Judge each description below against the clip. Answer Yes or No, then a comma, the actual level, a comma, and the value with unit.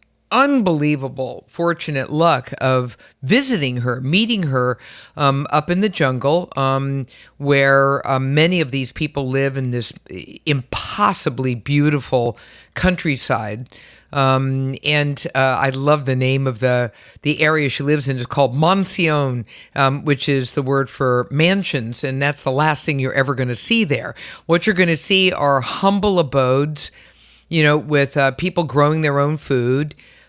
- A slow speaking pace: No, average, 155 wpm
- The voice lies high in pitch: No, medium, 140 Hz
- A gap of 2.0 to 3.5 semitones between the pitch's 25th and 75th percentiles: Yes, average, 2.8 semitones